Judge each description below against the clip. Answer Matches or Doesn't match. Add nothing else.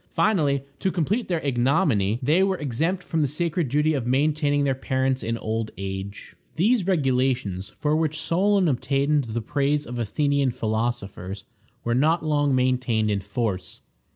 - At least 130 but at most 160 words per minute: Matches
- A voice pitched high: Doesn't match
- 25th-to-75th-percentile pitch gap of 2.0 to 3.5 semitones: Doesn't match